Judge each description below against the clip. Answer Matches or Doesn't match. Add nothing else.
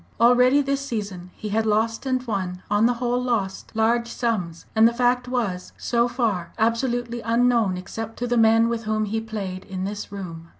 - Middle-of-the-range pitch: Doesn't match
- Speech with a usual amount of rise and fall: Matches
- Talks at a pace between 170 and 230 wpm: Matches